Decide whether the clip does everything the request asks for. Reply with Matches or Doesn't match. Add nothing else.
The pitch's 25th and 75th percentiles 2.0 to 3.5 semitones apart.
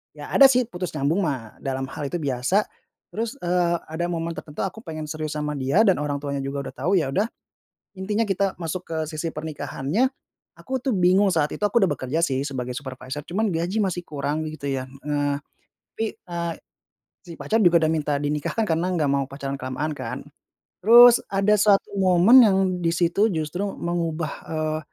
Doesn't match